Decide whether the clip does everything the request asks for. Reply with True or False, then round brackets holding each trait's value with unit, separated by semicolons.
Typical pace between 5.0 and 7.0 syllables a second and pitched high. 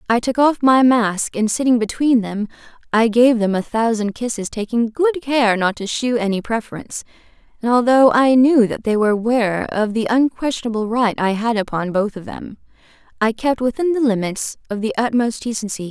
True (5.2 syllables/s; 230 Hz)